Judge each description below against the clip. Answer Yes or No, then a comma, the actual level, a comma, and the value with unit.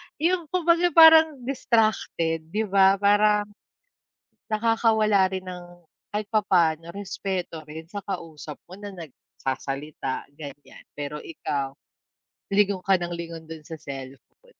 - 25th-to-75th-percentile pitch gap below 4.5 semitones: No, average, 5.1 semitones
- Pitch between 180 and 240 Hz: Yes, high, 190 Hz